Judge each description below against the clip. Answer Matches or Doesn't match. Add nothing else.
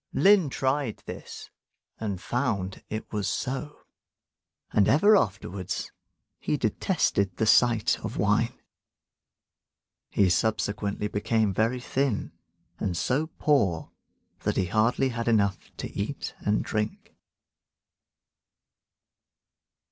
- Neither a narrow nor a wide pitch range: Matches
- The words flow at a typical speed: Doesn't match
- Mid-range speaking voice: Doesn't match